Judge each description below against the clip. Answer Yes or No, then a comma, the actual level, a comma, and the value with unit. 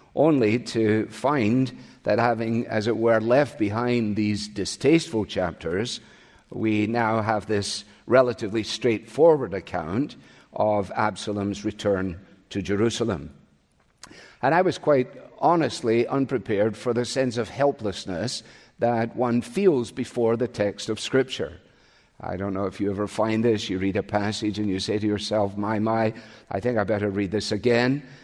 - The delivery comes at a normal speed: Yes, average, 150 wpm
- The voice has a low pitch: Yes, low, 110 Hz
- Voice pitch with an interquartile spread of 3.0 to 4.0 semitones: No, narrow, 2.5 semitones